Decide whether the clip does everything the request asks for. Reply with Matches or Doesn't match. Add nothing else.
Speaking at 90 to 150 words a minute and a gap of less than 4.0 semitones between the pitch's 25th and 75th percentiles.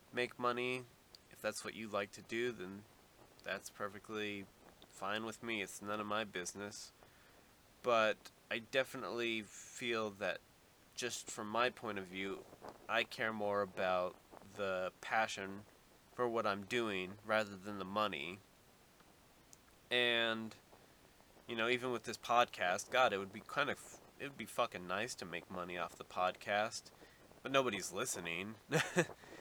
Matches